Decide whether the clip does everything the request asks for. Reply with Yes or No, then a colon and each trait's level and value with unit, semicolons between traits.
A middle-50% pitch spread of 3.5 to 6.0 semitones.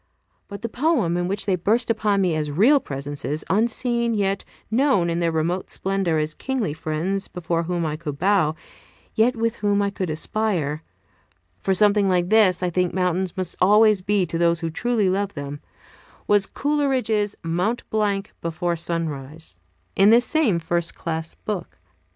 Yes: average, 4.3 semitones